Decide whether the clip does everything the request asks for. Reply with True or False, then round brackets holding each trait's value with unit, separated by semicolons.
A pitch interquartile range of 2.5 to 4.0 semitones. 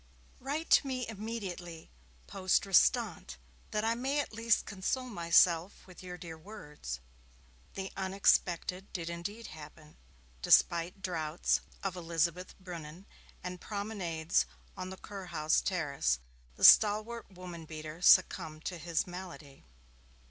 True (3.6 semitones)